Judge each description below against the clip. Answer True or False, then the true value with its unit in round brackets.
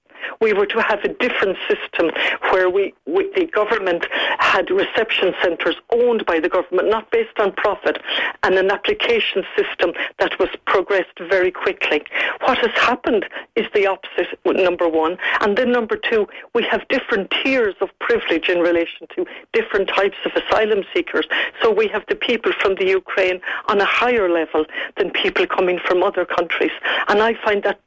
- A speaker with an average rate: True (170 wpm)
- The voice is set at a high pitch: True (215 Hz)